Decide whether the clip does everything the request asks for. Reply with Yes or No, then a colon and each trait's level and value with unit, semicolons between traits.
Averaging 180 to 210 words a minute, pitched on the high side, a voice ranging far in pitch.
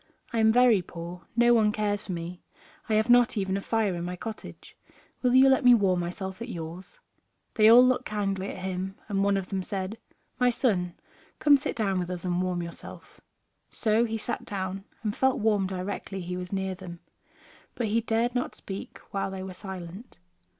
No: average, 200 wpm; high, 195 Hz; average, 3.6 semitones